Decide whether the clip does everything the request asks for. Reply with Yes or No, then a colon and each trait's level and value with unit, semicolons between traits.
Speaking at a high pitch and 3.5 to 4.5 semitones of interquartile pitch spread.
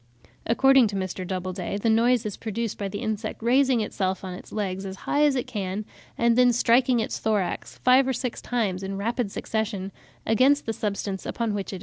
Yes: high, 220 Hz; average, 3.8 semitones